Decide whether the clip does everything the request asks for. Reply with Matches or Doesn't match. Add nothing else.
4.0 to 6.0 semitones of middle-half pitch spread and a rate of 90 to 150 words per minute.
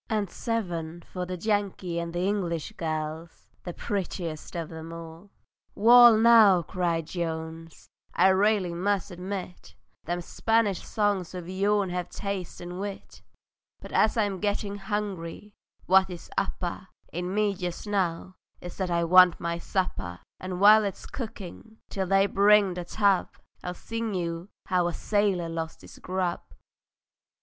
Doesn't match